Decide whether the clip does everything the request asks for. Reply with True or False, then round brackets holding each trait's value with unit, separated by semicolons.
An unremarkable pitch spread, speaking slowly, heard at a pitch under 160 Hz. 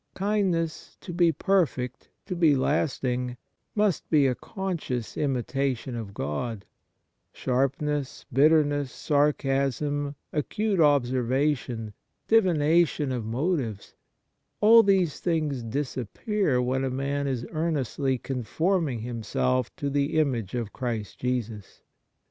True (4.2 semitones; 110 wpm; 140 Hz)